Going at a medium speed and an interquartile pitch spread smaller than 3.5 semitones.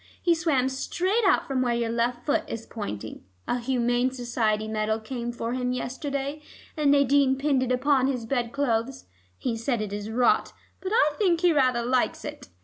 Yes: average, 185 wpm; average, 3.1 semitones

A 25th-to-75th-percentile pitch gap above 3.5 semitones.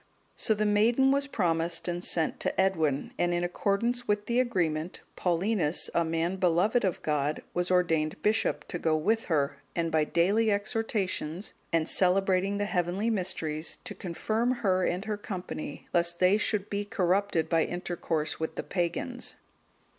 Yes: average, 3.9 semitones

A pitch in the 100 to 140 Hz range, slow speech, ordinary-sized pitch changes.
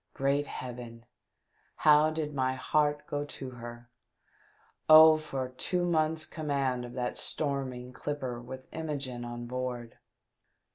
Yes: low, 135 Hz; slow, 130 wpm; average, 3.4 semitones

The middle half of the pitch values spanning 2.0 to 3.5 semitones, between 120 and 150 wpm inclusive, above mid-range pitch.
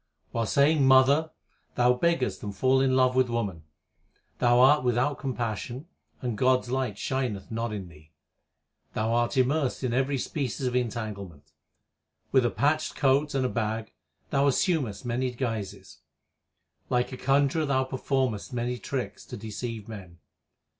No: average, 3.1 semitones; average, 140 wpm; low, 125 Hz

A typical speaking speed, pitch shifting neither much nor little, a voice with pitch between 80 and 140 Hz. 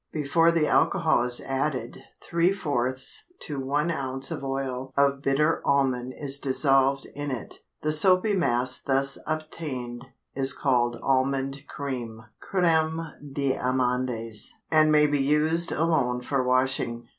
No: slow, 130 wpm; average, 3.0 semitones; low, 135 Hz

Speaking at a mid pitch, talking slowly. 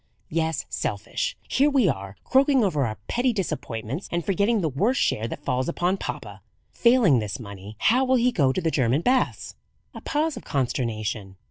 No: medium, 165 Hz; average, 175 wpm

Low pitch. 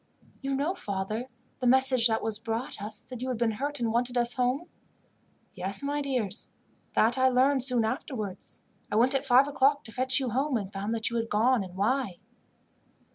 No: high, 245 Hz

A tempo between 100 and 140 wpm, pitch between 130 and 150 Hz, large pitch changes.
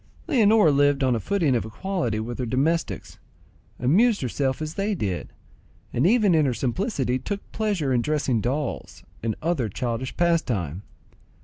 No: average, 150 wpm; medium, 140 Hz; wide, 7.1 semitones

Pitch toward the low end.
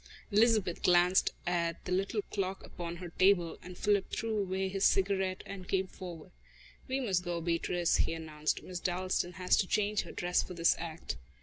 No: medium, 185 Hz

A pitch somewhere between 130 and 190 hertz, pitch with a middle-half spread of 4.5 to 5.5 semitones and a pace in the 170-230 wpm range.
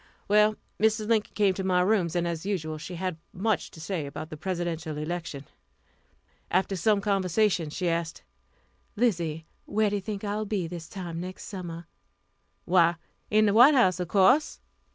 No: medium, 185 Hz; average, 3.7 semitones; average, 175 wpm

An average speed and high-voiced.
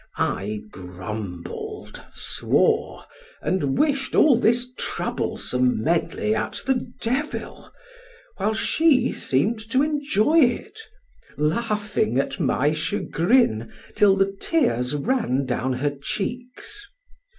No: slow, 100 wpm; high, 205 Hz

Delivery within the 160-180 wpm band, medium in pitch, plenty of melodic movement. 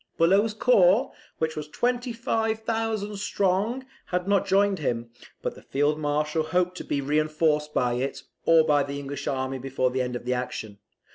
Yes: average, 165 wpm; medium, 155 Hz; wide, 6.5 semitones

